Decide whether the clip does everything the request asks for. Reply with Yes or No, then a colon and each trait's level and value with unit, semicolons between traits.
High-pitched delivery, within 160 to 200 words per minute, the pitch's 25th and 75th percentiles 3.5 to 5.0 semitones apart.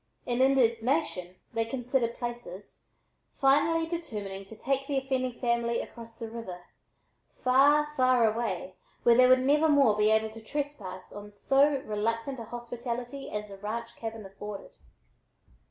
No: high, 235 Hz; average, 140 wpm; average, 3.8 semitones